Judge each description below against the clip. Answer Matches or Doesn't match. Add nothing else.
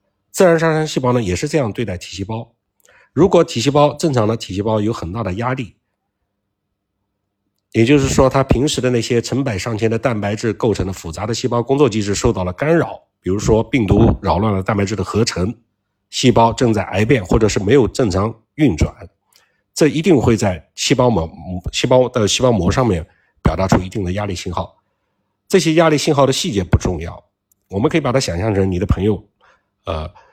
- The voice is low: Matches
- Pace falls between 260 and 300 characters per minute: Matches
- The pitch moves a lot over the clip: Doesn't match